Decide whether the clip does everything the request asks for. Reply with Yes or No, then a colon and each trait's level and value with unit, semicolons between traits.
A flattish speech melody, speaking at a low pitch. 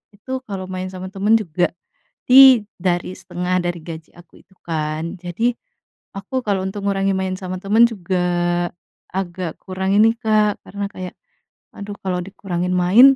No: narrow, 2.3 semitones; medium, 185 Hz